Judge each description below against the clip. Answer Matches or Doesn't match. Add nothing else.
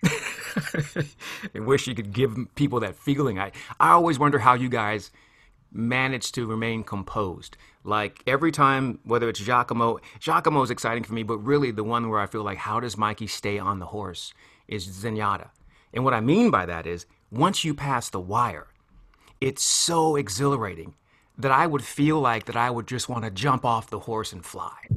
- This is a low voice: Matches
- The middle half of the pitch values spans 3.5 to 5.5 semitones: Matches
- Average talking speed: Matches